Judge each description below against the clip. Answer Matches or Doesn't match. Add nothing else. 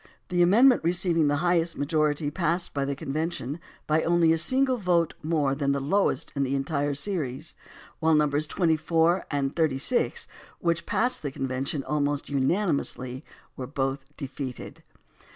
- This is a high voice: Doesn't match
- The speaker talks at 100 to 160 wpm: Matches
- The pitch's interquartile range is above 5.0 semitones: Doesn't match